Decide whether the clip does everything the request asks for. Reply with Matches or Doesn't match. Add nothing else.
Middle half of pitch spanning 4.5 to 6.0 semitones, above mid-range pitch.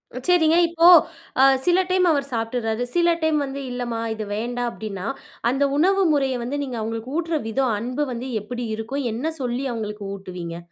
Matches